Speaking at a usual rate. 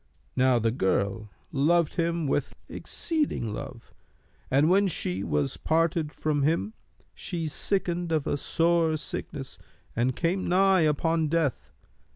No: slow, 130 wpm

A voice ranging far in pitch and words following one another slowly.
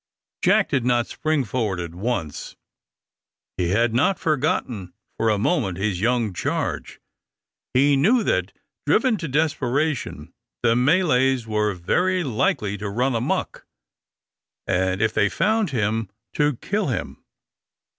Yes: wide, 5.9 semitones; slow, 130 wpm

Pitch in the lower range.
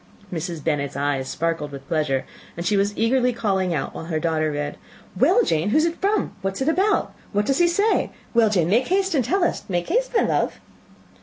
No: high, 195 Hz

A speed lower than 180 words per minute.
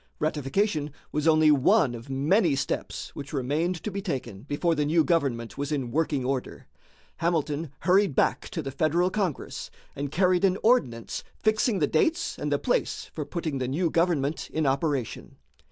Yes: average, 170 wpm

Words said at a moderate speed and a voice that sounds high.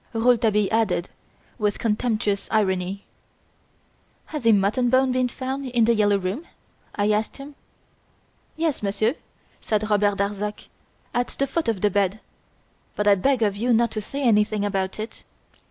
Yes: average, 155 wpm; high, 215 Hz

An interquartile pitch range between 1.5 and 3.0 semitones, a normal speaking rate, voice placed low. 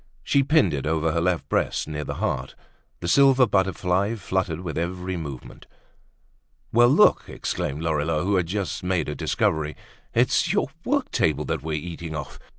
No: average, 4.1 semitones; average, 170 wpm; very low, 85 Hz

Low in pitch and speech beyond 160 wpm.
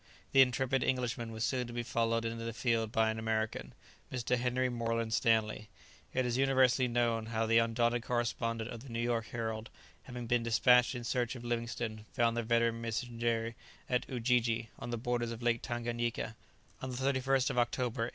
Yes: low, 120 Hz; average, 185 wpm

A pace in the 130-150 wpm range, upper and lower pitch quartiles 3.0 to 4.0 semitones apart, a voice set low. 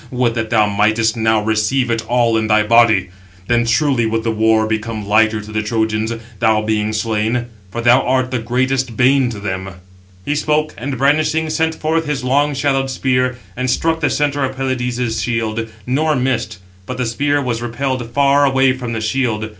No: average, 185 wpm; average, 3.3 semitones; low, 120 Hz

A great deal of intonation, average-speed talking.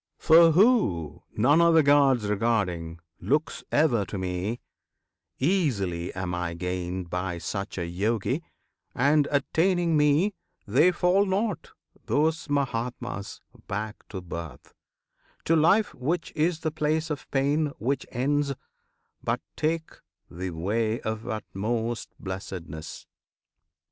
No: wide, 8.8 semitones; slow, 115 wpm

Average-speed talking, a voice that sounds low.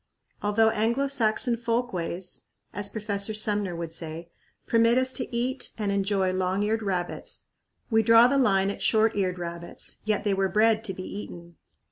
No: average, 165 wpm; high, 205 Hz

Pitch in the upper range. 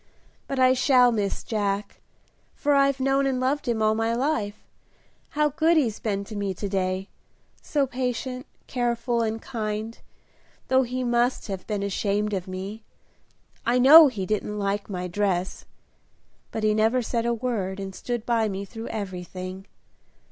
Yes: high, 225 Hz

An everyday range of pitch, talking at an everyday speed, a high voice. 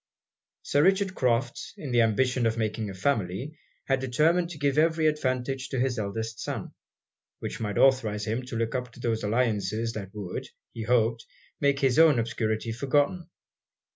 No: average, 4.0 semitones; average, 170 wpm; low, 125 Hz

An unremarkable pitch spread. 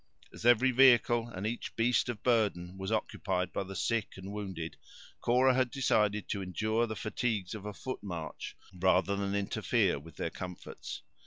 Yes: average, 3.9 semitones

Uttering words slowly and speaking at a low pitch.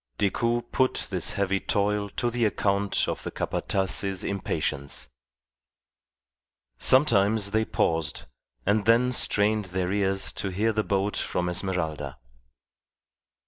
Yes: slow, 115 wpm; low, 100 Hz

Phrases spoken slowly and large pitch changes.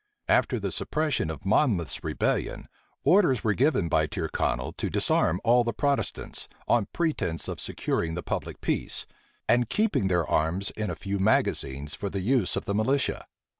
No: average, 165 wpm; wide, 7.1 semitones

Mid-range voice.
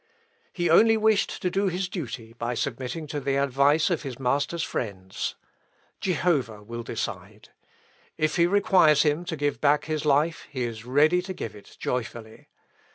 Yes: medium, 145 Hz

